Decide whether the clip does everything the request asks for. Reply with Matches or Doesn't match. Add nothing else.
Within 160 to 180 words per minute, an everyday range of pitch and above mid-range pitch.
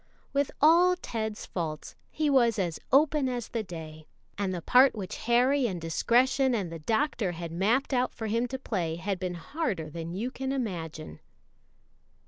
Doesn't match